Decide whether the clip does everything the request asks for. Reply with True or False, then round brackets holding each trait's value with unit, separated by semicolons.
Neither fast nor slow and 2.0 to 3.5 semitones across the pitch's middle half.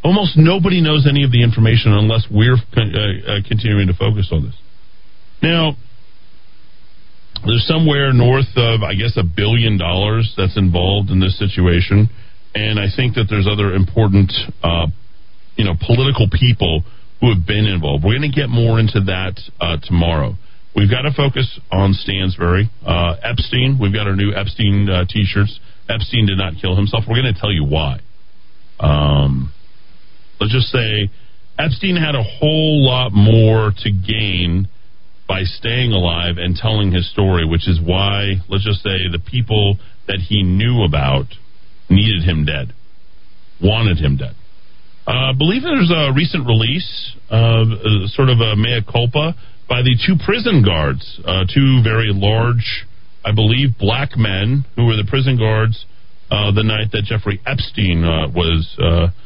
False (160 wpm; 3.9 semitones)